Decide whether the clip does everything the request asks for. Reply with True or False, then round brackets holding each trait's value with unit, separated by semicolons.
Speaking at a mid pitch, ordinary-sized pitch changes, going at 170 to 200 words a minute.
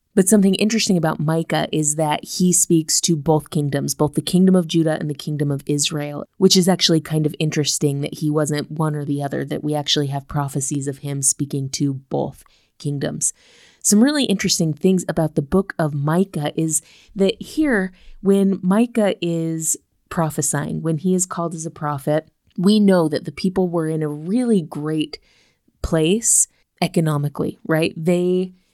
True (160 Hz; 3.8 semitones; 175 wpm)